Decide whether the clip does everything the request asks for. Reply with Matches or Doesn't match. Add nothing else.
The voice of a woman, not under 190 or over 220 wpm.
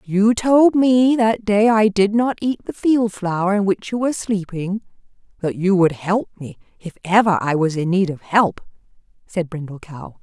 Matches